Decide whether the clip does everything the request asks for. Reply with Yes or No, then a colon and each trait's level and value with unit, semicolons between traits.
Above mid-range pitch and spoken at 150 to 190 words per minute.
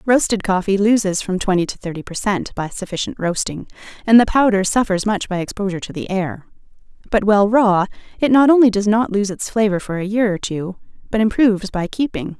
No: high, 200 Hz; fast, 205 wpm